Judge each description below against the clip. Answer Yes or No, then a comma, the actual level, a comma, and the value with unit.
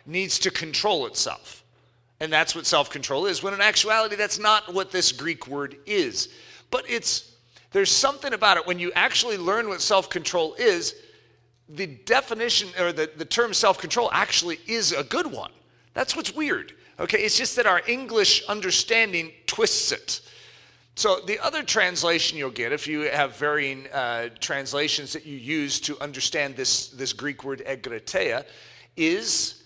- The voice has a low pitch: No, medium, 180 Hz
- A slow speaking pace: No, average, 160 wpm